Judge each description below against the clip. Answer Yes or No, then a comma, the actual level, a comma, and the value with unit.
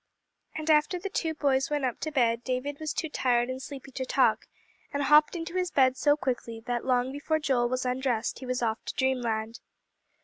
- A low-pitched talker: No, very high, 265 Hz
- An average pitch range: Yes, average, 3.3 semitones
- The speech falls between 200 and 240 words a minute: Yes, fast, 205 wpm